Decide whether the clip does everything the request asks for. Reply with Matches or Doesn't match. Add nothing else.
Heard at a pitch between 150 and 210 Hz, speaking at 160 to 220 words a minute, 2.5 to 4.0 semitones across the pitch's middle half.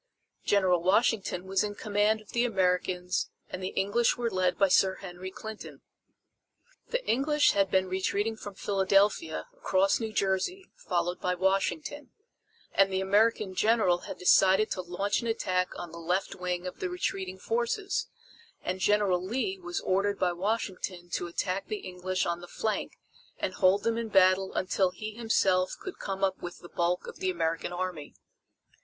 Matches